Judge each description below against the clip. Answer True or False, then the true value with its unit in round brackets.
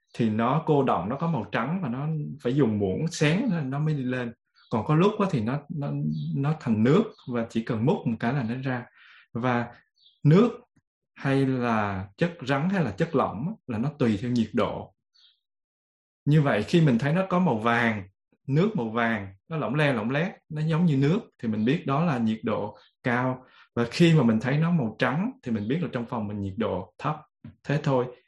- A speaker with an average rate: True (215 wpm)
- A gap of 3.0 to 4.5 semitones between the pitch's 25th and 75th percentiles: False (5.1 semitones)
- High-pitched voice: False (130 Hz)